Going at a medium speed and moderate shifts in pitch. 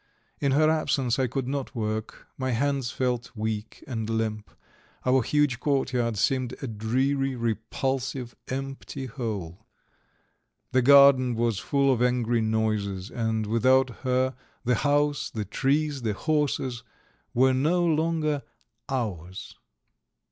No: slow, 125 wpm; average, 3.5 semitones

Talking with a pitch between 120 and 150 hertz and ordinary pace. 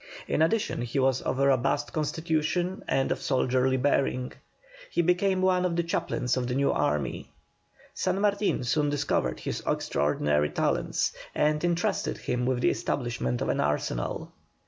Yes: medium, 140 Hz; average, 155 wpm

